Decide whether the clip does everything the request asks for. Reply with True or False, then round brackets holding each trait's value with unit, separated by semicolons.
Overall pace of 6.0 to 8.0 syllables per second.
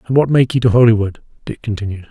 True (7.0 syllables/s)